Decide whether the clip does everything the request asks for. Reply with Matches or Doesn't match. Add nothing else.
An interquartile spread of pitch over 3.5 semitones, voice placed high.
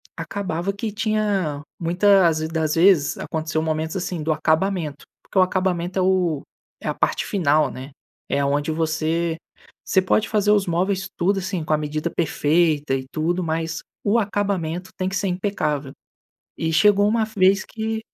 Doesn't match